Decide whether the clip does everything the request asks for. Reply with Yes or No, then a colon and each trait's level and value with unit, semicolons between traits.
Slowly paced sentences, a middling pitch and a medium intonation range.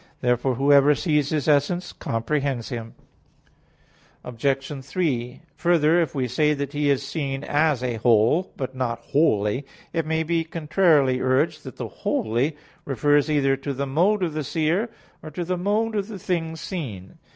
No: average, 160 wpm; medium, 145 Hz; average, 3.7 semitones